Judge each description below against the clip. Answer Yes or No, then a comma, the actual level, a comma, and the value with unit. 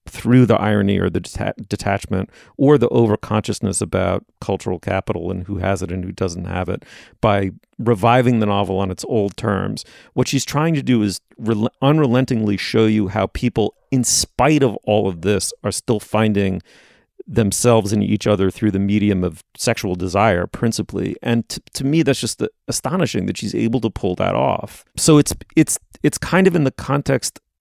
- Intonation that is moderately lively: Yes, average, 3.8 semitones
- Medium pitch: No, low, 105 Hz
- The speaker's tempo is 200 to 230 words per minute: No, average, 180 wpm